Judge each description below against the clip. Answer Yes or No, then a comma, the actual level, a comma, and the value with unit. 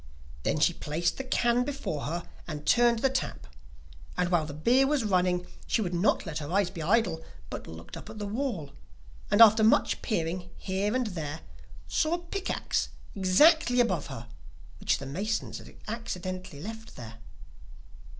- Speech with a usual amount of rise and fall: No, wide, 6.3 semitones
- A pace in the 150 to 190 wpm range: Yes, average, 170 wpm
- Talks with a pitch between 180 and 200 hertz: Yes, high, 190 Hz